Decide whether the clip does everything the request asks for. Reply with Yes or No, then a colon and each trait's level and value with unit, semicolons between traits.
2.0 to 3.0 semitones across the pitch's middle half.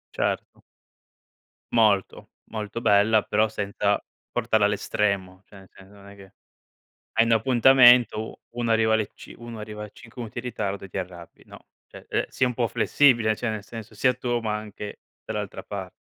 Yes: narrow, 2.5 semitones